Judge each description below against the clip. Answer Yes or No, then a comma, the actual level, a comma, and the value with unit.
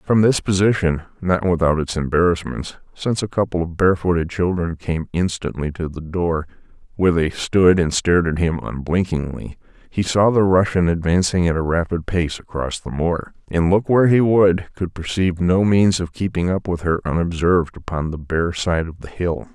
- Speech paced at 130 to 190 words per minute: Yes, average, 180 wpm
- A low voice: Yes, very low, 85 Hz